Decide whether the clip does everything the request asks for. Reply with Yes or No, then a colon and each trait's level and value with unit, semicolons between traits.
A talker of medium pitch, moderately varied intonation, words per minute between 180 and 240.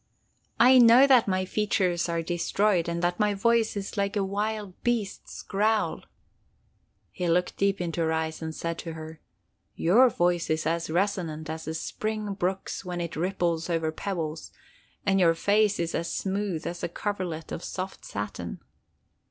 No: medium, 180 Hz; average, 3.6 semitones; average, 165 wpm